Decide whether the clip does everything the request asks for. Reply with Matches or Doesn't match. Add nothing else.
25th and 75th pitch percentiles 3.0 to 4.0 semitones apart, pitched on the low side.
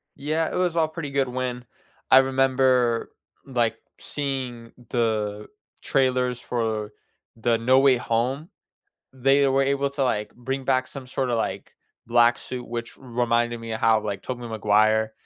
Doesn't match